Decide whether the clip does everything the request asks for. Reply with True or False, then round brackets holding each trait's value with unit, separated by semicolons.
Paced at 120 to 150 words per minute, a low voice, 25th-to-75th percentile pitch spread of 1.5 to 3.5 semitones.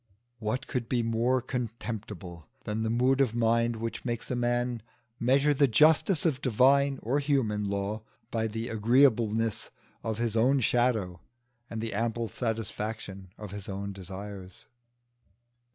True (140 wpm; 115 Hz; 3.0 semitones)